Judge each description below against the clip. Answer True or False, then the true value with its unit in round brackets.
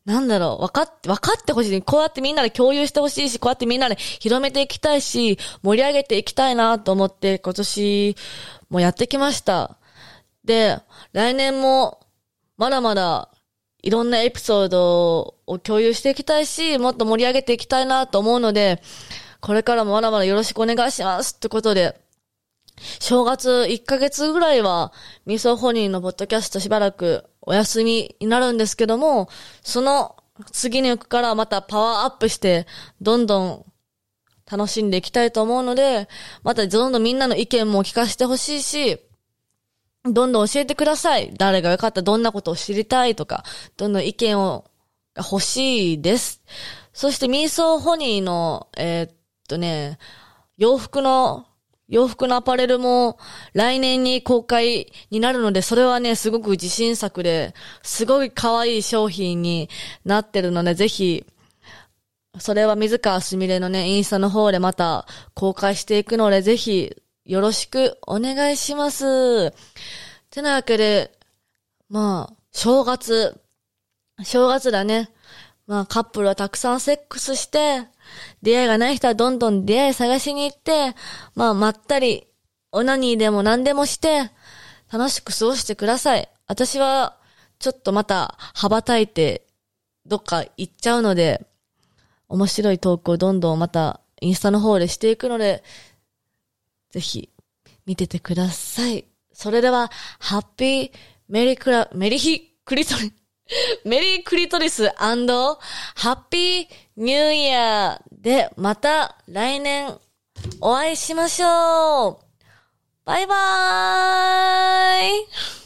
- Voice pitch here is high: True (225 Hz)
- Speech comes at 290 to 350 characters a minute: True (300 characters per minute)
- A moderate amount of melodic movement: True (5.0 semitones)